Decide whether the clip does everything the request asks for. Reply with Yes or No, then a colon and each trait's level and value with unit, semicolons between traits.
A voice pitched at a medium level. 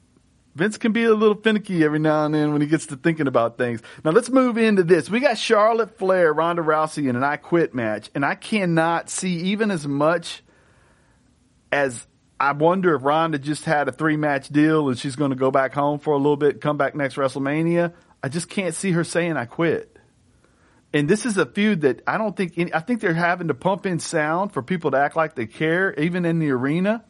Yes: medium, 160 Hz